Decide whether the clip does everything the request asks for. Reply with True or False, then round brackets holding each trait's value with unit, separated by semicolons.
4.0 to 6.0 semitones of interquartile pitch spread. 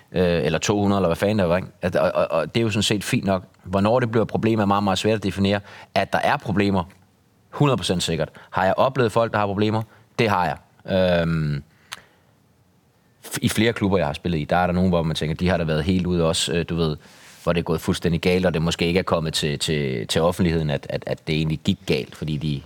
False (3.6 semitones)